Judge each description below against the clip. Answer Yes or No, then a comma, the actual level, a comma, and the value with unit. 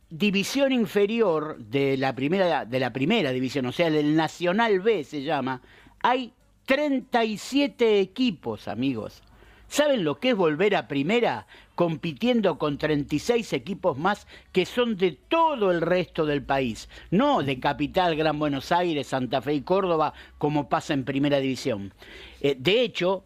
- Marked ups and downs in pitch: Yes, wide, 6.4 semitones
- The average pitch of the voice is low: No, medium, 165 Hz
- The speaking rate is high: No, average, 145 wpm